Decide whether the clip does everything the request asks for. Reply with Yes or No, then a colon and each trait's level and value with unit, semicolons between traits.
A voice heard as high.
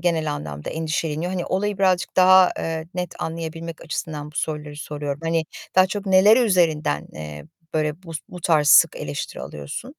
No: medium, 165 Hz